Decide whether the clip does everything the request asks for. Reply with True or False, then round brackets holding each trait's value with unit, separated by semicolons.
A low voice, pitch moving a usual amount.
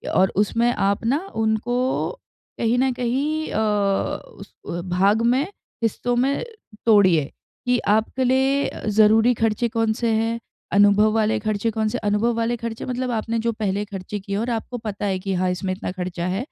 False (220 Hz; 3.0 semitones)